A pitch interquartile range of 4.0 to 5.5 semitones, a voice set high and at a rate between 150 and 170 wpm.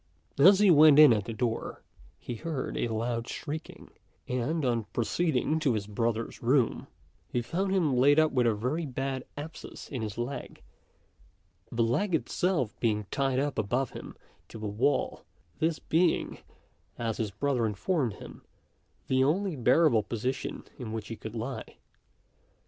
No: average, 5.0 semitones; low, 125 Hz; average, 155 wpm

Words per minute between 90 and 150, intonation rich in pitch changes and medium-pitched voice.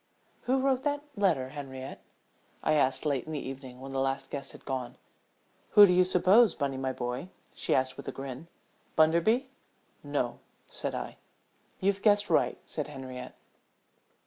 No: average, 160 wpm; wide, 6.8 semitones; medium, 145 Hz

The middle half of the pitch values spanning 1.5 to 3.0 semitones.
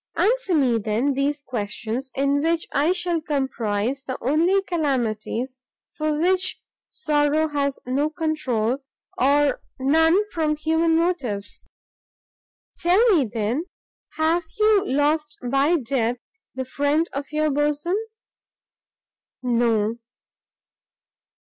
No: average, 4.0 semitones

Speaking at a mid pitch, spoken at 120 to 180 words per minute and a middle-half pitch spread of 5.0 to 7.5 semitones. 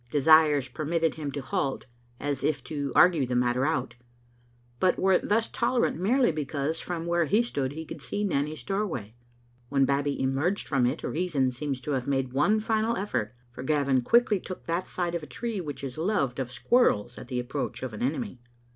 No: medium, 150 Hz; average, 190 wpm; wide, 5.4 semitones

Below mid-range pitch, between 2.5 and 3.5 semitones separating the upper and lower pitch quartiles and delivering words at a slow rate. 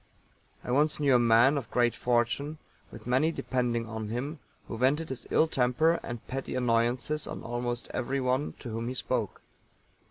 No: low, 125 Hz; average, 2.8 semitones; average, 165 wpm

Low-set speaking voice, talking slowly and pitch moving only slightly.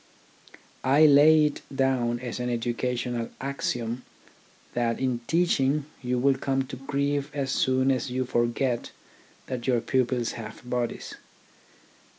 Yes: low, 130 Hz; slow, 130 wpm; narrow, 2.2 semitones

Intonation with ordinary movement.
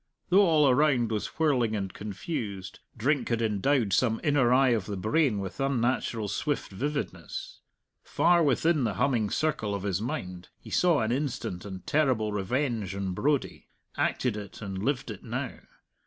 No: wide, 5.8 semitones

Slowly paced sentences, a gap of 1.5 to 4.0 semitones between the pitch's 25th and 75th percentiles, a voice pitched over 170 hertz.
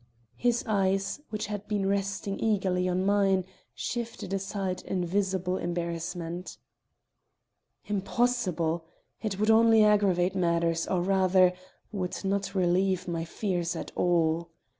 Yes: slow, 120 wpm; narrow, 2.4 semitones; high, 190 Hz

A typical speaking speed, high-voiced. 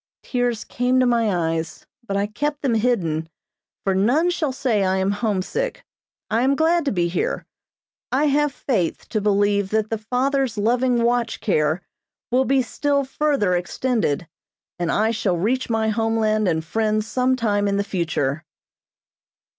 Yes: average, 160 wpm; high, 220 Hz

